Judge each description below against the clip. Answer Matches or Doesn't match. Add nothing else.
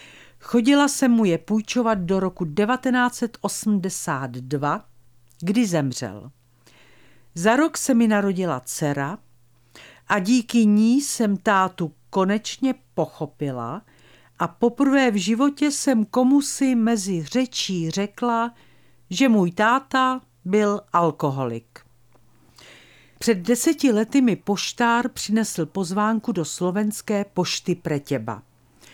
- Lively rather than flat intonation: Matches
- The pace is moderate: Doesn't match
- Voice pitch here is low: Doesn't match